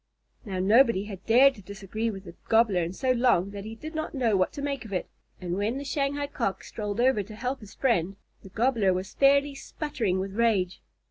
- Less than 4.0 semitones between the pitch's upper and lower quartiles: No, wide, 5.4 semitones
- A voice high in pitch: Yes, high, 220 Hz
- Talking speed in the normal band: No, fast, 215 wpm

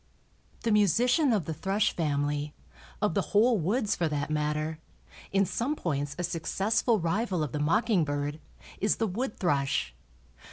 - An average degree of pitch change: No, wide, 6.2 semitones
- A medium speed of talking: Yes, average, 155 wpm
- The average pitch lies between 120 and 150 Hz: No, medium, 175 Hz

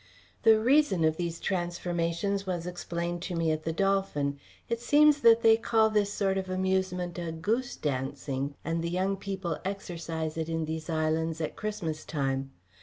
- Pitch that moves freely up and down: No, average, 3.5 semitones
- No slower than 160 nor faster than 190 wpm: Yes, average, 170 wpm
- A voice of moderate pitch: Yes, medium, 175 Hz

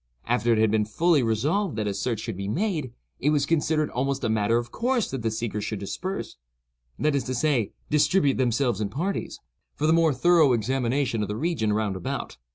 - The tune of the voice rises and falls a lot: Yes, wide, 5.9 semitones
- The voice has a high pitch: No, low, 125 Hz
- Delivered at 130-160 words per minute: No, average, 195 wpm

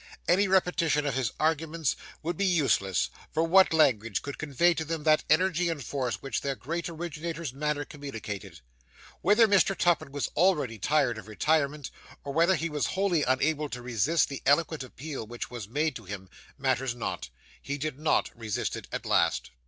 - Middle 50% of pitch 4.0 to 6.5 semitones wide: Yes, average, 4.4 semitones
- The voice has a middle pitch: Yes, medium, 150 Hz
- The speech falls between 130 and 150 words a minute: No, average, 180 wpm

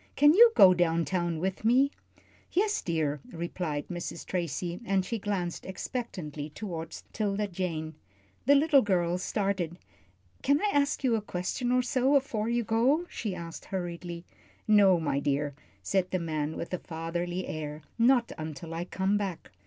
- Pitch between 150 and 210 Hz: Yes, medium, 185 Hz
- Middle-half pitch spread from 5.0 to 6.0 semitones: Yes, wide, 5.4 semitones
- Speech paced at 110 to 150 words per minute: No, average, 160 wpm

